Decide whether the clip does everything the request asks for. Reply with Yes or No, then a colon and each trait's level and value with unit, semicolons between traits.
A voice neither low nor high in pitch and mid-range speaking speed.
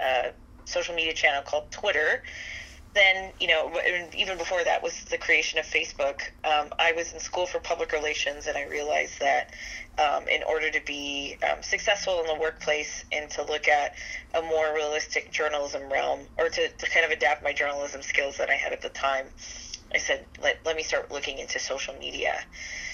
Yes: medium, 155 Hz; average, 190 wpm